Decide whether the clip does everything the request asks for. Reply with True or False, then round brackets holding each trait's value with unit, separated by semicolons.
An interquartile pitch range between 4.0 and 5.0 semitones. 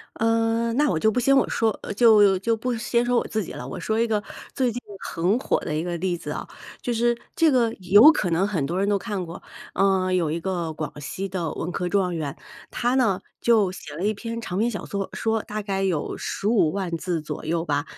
True (4.5 semitones)